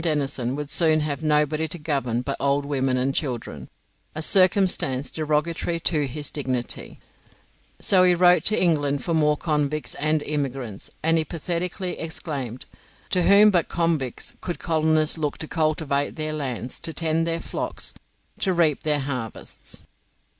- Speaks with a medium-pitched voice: Yes, medium, 155 Hz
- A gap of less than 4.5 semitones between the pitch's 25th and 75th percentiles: Yes, average, 2.9 semitones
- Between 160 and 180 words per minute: No, average, 150 wpm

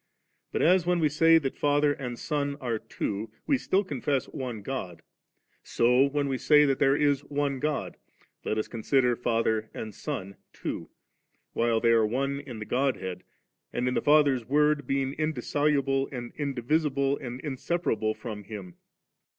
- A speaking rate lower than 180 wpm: Yes, average, 160 wpm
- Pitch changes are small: No, average, 3.8 semitones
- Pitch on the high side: No, low, 135 Hz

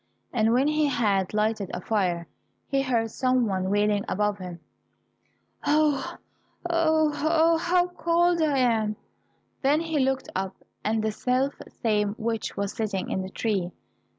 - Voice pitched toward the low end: No, high, 230 Hz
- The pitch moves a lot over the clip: Yes, wide, 6.4 semitones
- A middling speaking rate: Yes, average, 150 wpm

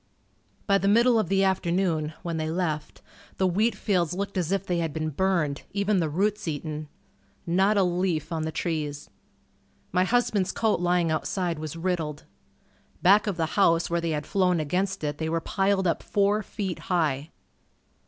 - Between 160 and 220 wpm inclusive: Yes, average, 175 wpm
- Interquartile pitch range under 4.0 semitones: Yes, average, 3.5 semitones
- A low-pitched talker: No, medium, 175 Hz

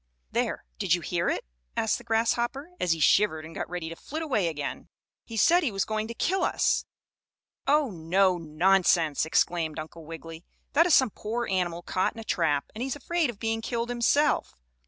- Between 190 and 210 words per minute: Yes, average, 195 wpm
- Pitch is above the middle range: Yes, high, 210 Hz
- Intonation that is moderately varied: No, wide, 6.5 semitones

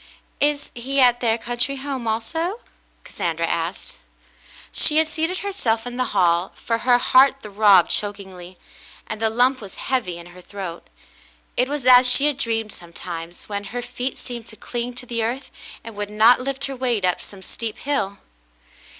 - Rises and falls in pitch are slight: No, average, 4.5 semitones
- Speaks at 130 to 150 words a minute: No, average, 175 wpm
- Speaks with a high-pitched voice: Yes, high, 230 Hz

